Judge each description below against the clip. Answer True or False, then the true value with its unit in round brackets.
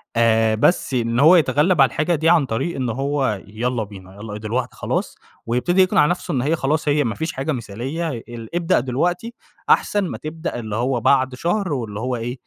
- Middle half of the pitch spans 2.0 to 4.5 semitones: False (5.6 semitones)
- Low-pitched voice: True (130 Hz)